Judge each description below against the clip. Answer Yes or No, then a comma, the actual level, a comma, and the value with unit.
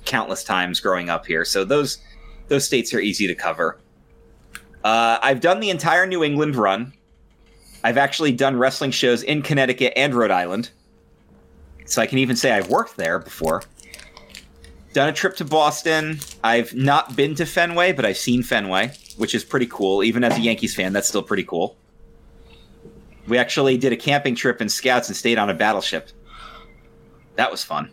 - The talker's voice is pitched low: Yes, low, 120 Hz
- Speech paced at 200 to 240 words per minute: No, average, 180 wpm